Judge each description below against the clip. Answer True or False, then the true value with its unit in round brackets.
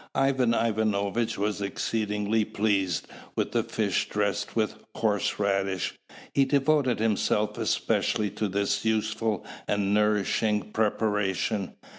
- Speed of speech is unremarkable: False (110 wpm)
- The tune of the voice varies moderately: False (1.8 semitones)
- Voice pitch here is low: True (105 Hz)